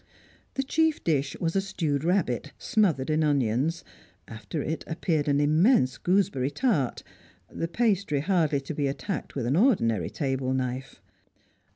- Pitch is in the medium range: Yes, medium, 150 Hz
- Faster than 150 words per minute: No, average, 145 wpm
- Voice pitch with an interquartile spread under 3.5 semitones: No, wide, 5.5 semitones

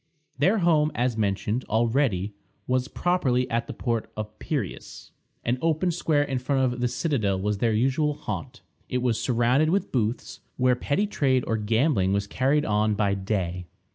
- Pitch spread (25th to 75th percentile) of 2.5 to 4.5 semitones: No, average, 5.0 semitones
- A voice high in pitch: No, low, 125 Hz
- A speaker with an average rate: Yes, average, 170 wpm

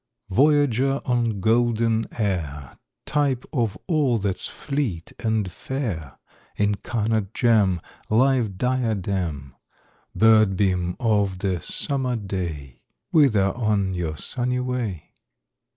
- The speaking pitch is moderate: No, low, 110 Hz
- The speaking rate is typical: No, slow, 100 wpm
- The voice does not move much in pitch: No, average, 4.9 semitones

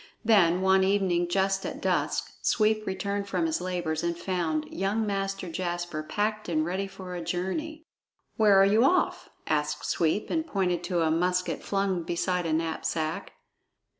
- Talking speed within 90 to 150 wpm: No, average, 160 wpm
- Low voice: No, medium, 185 Hz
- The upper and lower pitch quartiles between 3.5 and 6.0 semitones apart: No, average, 2.7 semitones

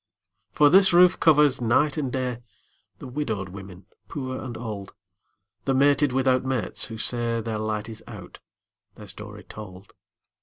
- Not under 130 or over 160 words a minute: Yes, average, 150 wpm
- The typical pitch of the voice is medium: No, low, 120 Hz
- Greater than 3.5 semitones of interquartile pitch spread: Yes, average, 4.1 semitones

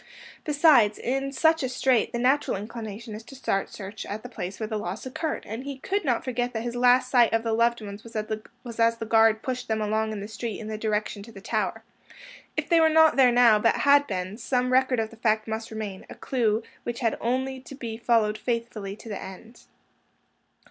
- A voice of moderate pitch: No, high, 230 Hz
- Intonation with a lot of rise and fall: No, average, 2.8 semitones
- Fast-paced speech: Yes, fast, 215 wpm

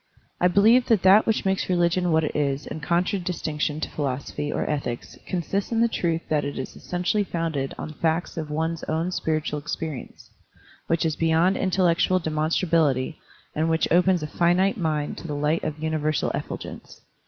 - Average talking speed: Yes, average, 175 wpm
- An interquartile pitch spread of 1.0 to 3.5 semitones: Yes, average, 2.9 semitones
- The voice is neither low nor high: Yes, medium, 165 Hz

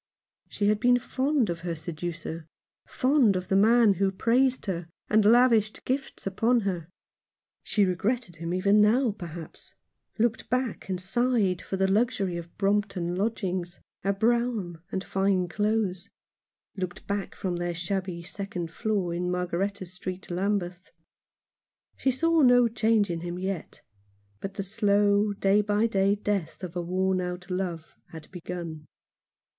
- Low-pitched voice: No, high, 195 Hz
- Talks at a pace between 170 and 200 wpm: No, average, 150 wpm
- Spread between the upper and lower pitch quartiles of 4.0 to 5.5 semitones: No, average, 3.4 semitones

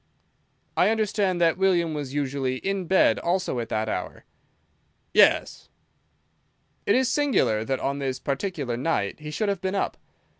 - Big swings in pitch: Yes, wide, 6.4 semitones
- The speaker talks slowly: No, average, 150 wpm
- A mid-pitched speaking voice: Yes, medium, 165 Hz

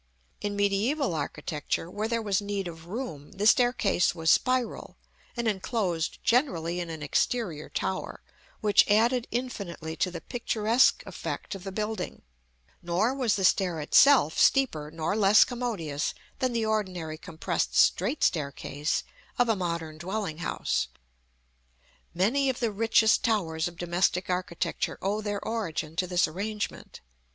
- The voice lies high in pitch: Yes, high, 195 Hz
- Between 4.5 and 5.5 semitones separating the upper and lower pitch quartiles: Yes, average, 5.0 semitones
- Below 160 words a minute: Yes, average, 140 wpm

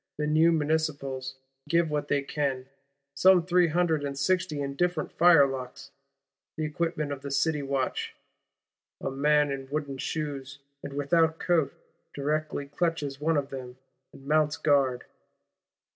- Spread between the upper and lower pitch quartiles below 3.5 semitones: Yes, narrow, 2.5 semitones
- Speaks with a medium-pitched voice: Yes, medium, 145 Hz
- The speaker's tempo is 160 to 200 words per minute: No, slow, 135 wpm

